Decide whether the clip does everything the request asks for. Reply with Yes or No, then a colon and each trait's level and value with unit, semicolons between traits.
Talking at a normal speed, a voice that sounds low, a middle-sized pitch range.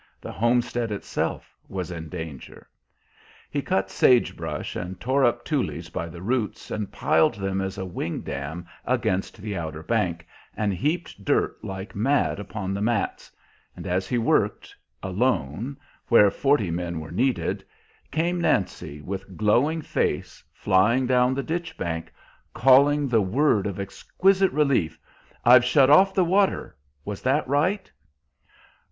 No: average, 145 wpm; low, 105 Hz; wide, 6.4 semitones